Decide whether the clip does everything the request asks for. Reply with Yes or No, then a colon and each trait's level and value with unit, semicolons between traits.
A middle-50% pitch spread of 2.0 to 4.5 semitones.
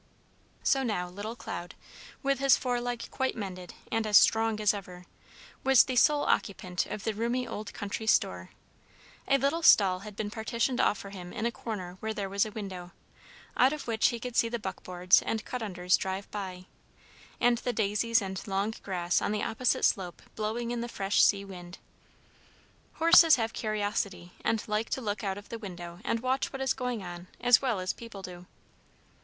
Yes: average, 3.9 semitones